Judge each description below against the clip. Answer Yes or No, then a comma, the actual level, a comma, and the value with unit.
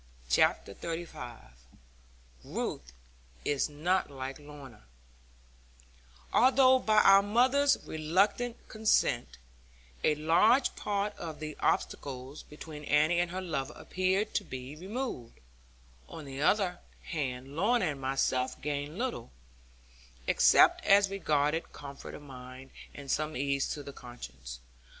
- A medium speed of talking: No, slow, 120 wpm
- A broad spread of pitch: Yes, wide, 6.3 semitones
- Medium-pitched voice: Yes, medium, 155 Hz